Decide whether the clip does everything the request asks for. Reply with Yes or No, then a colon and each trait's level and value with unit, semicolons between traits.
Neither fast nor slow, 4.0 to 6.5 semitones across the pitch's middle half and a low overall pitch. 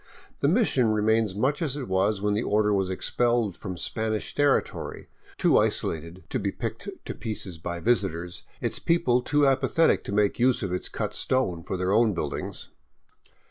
Yes: average, 175 wpm; average, 5.0 semitones; low, 110 Hz